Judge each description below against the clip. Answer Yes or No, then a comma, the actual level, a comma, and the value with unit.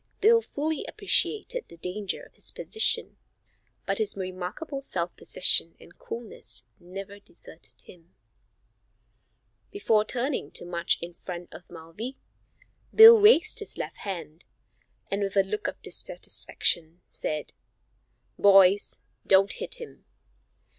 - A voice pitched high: Yes, high, 195 Hz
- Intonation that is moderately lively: No, wide, 8.8 semitones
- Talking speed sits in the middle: No, slow, 120 wpm